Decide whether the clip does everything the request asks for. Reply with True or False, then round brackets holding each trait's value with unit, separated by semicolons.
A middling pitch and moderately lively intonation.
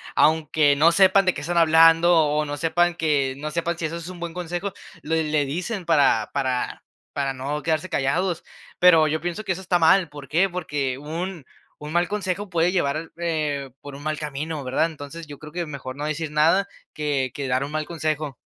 True (155 Hz; 3.0 semitones)